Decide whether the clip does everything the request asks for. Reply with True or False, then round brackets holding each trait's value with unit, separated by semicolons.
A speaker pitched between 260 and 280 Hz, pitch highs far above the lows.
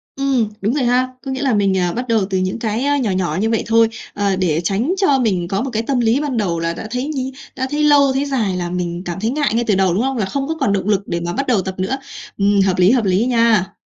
False (225 Hz; 5.7 semitones)